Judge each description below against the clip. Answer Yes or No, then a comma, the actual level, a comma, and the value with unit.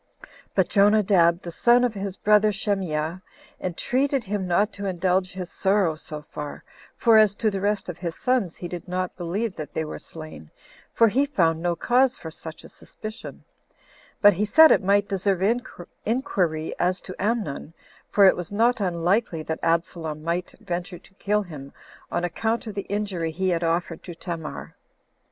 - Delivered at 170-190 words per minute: Yes, average, 175 wpm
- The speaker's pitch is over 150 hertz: Yes, medium, 185 Hz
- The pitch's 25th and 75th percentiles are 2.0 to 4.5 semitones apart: Yes, average, 3.7 semitones